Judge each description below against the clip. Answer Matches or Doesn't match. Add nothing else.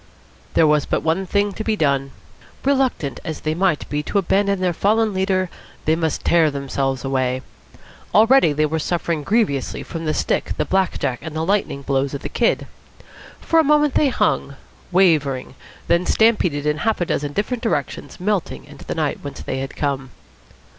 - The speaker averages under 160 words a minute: Doesn't match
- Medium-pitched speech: Matches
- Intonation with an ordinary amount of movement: Doesn't match